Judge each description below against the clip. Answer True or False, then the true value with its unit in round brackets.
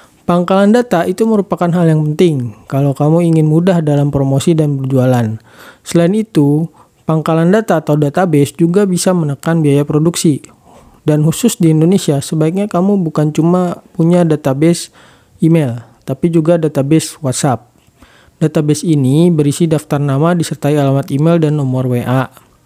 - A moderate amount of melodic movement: True (3.3 semitones)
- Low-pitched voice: False (160 Hz)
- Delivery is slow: False (140 wpm)